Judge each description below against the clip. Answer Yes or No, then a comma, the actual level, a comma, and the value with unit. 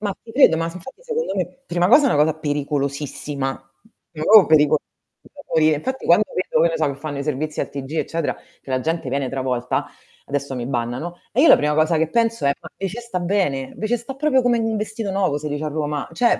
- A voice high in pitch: No, medium, 160 Hz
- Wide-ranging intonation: Yes, wide, 7.0 semitones